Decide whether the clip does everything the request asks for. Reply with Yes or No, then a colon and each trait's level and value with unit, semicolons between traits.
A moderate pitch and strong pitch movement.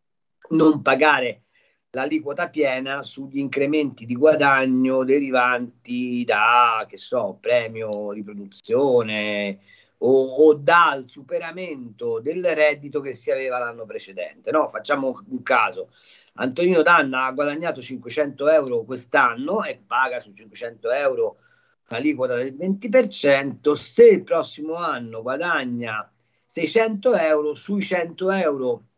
Yes: medium, 150 Hz; wide, 7.9 semitones